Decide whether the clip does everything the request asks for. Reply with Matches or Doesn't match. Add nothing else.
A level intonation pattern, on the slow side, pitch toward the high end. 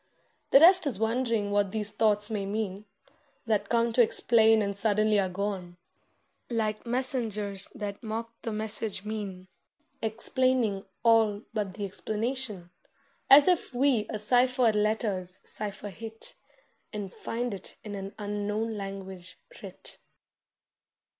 Matches